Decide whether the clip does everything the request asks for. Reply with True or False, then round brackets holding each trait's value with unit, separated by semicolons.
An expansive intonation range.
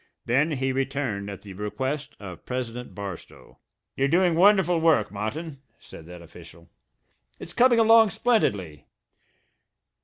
True (8.6 semitones)